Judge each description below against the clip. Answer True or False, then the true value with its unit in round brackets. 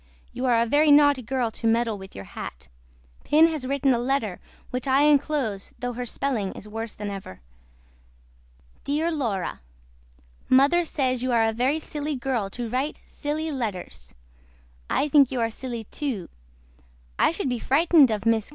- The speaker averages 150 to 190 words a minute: True (170 wpm)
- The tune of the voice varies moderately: True (4.3 semitones)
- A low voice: False (255 Hz)